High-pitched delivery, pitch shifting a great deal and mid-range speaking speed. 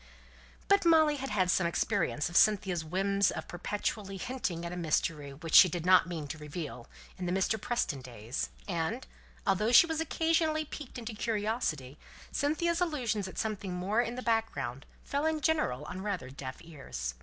Yes: high, 195 Hz; wide, 7.2 semitones; average, 175 wpm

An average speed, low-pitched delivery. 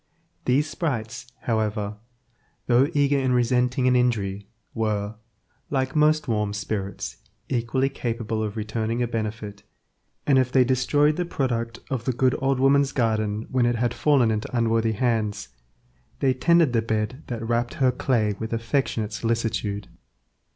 Yes: average, 145 wpm; low, 120 Hz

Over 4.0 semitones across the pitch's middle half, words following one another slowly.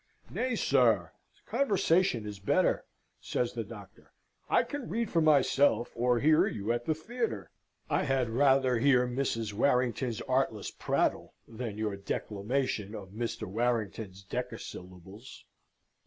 Yes: average, 4.7 semitones; slow, 125 wpm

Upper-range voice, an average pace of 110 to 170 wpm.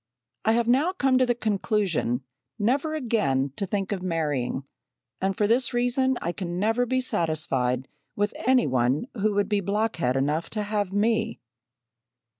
Yes: high, 205 Hz; average, 160 wpm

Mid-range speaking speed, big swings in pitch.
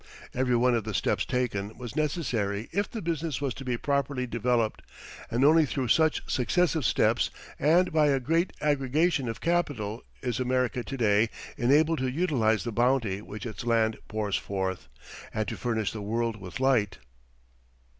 No: average, 165 wpm; average, 4.7 semitones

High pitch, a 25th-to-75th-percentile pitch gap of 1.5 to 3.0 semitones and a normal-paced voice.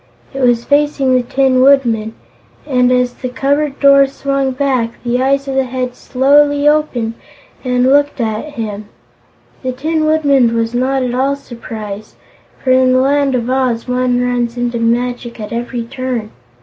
Yes: very high, 255 Hz; narrow, 2.4 semitones; average, 160 wpm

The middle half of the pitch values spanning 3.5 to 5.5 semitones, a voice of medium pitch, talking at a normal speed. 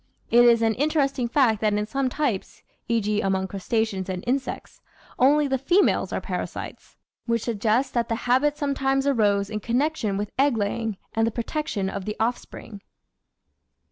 No: average, 4.4 semitones; high, 230 Hz; average, 160 wpm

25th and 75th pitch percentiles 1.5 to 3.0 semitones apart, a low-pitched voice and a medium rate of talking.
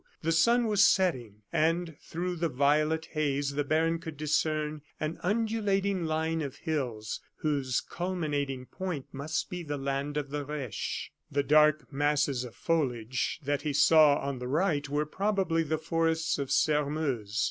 No: average, 2.7 semitones; medium, 150 Hz; average, 155 wpm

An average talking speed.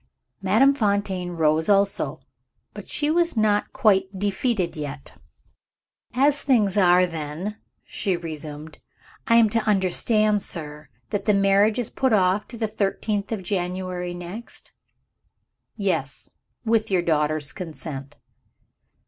No: slow, 125 wpm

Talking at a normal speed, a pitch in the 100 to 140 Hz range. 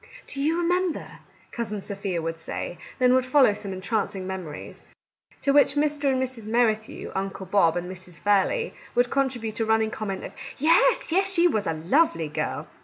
No: average, 185 wpm; high, 220 Hz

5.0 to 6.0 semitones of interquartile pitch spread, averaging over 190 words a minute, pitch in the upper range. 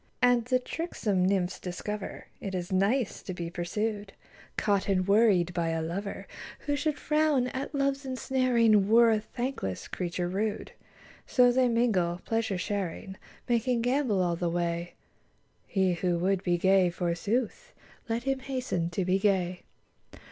No: wide, 5.4 semitones; average, 150 wpm; high, 200 Hz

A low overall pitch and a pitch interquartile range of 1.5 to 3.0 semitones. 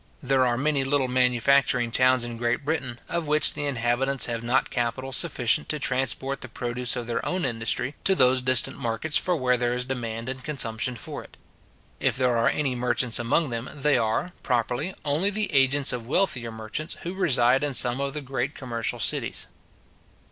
Yes: low, 130 Hz; average, 2.7 semitones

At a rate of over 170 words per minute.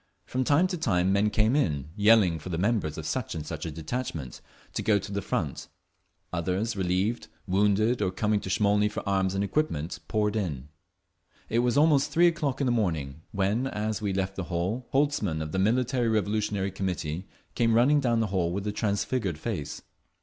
Yes: average, 190 wpm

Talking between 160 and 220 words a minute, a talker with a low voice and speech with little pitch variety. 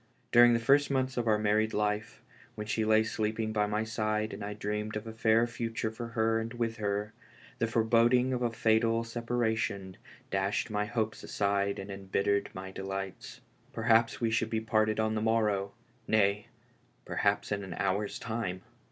Yes: average, 180 wpm; low, 110 Hz; narrow, 1.7 semitones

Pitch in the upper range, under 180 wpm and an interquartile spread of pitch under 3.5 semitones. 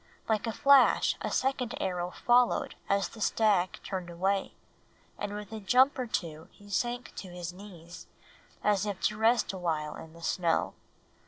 No: high, 200 Hz; average, 165 wpm; average, 4.2 semitones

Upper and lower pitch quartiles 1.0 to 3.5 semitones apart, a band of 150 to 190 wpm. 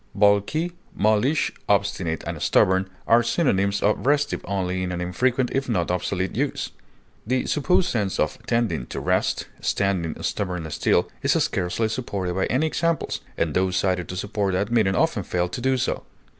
No: average, 5.1 semitones; average, 165 wpm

